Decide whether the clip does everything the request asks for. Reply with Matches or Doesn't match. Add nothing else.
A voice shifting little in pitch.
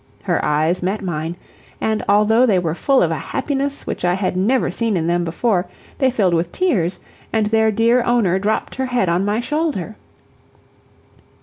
Doesn't match